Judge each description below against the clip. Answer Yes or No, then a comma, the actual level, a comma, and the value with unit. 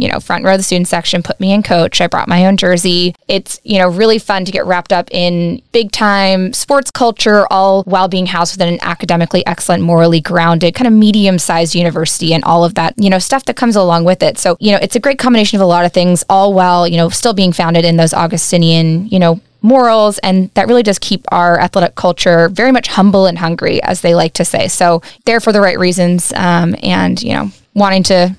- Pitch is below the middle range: No, medium, 180 Hz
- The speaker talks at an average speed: No, fast, 235 wpm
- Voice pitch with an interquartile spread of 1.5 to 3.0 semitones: Yes, average, 2.7 semitones